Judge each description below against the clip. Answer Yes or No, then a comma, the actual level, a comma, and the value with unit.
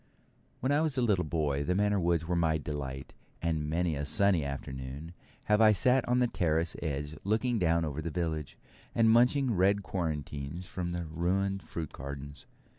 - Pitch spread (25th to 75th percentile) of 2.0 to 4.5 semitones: No, average, 5.1 semitones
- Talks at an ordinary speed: Yes, average, 180 wpm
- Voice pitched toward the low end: Yes, very low, 85 Hz